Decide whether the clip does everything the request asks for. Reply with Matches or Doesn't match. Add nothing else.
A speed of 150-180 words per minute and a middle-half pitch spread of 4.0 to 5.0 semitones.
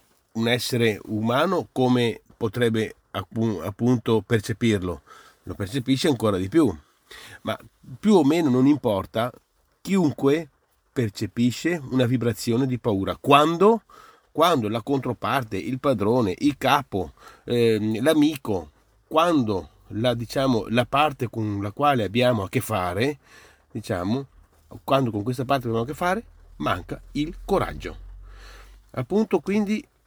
Doesn't match